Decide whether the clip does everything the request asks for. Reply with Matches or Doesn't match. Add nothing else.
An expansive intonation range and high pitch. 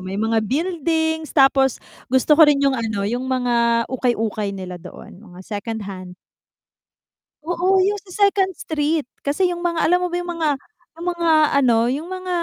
Matches